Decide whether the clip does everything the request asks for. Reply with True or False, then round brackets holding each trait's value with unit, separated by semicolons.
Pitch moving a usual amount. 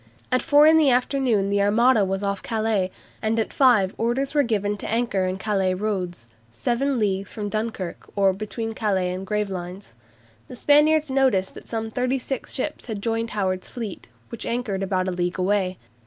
True (4.1 semitones)